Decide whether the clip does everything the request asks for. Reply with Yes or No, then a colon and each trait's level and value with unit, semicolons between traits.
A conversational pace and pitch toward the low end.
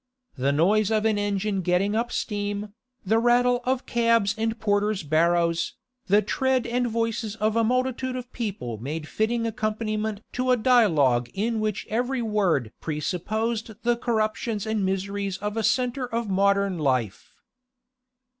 No: average, 145 wpm; high, 215 Hz